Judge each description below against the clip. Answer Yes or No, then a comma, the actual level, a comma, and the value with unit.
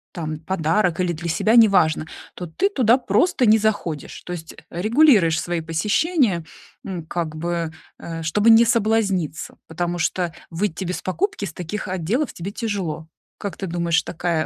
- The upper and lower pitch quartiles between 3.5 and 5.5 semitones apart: Yes, average, 4.7 semitones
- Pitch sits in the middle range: Yes, medium, 180 Hz